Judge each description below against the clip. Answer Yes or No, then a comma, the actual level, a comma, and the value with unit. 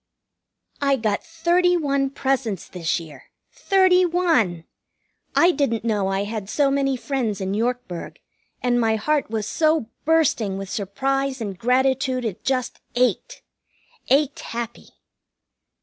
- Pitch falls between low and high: No, very high, 250 Hz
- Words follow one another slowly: Yes, slow, 130 wpm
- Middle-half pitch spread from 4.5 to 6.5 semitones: Yes, average, 5.0 semitones